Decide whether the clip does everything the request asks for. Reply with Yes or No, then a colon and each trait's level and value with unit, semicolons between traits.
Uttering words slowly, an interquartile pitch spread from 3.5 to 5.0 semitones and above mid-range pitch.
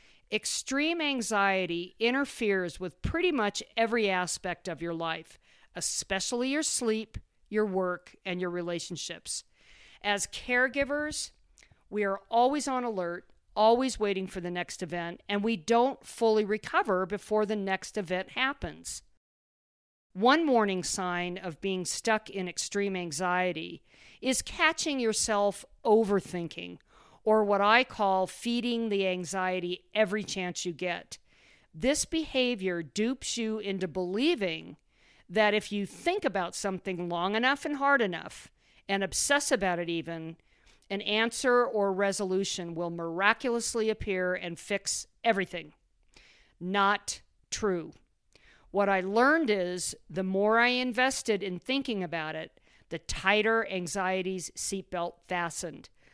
Yes: slow, 125 wpm; average, 4.2 semitones; high, 200 Hz